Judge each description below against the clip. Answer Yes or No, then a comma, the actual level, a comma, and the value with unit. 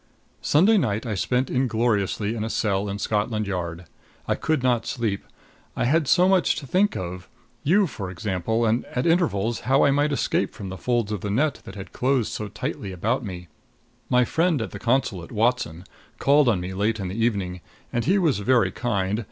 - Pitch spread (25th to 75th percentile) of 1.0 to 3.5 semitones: No, average, 5.0 semitones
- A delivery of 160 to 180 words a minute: No, average, 195 wpm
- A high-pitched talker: No, low, 115 Hz